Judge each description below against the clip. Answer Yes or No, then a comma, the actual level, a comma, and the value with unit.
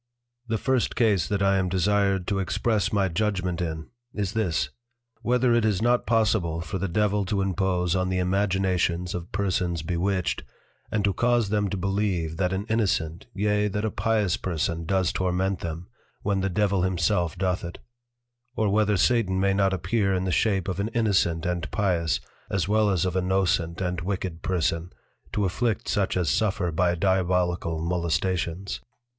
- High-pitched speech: No, very low, 95 Hz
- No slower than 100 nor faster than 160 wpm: No, average, 175 wpm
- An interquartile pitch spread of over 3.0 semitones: No, narrow, 2.6 semitones